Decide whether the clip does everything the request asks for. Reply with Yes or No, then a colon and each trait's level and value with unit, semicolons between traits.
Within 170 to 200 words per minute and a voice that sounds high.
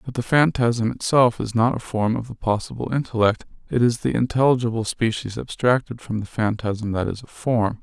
No: average, 190 wpm; low, 115 Hz